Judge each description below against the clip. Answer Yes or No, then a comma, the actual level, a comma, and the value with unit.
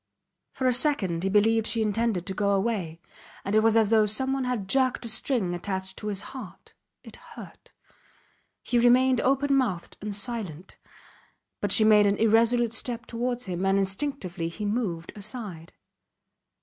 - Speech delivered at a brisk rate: No, average, 160 wpm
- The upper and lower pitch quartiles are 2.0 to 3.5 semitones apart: No, average, 4.0 semitones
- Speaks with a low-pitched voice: No, high, 215 Hz